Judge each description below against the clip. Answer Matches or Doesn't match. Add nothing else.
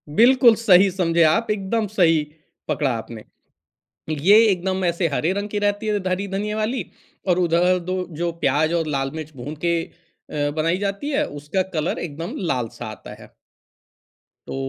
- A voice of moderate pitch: Matches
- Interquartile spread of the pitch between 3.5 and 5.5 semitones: Matches